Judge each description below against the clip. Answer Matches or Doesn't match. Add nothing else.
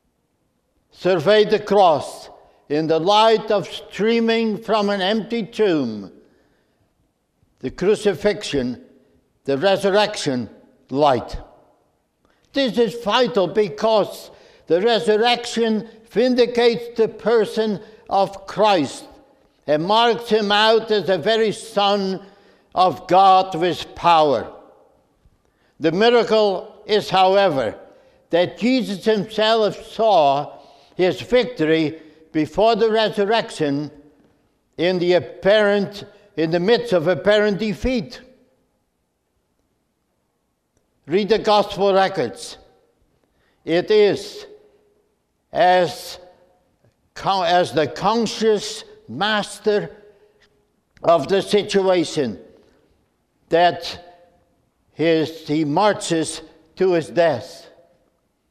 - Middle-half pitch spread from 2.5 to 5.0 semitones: Matches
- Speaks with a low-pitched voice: Doesn't match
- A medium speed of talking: Doesn't match